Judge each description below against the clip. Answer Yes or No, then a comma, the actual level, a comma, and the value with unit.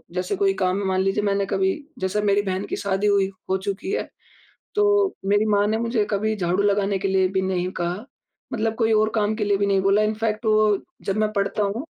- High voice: Yes, high, 200 Hz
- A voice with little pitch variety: Yes, narrow, 1.8 semitones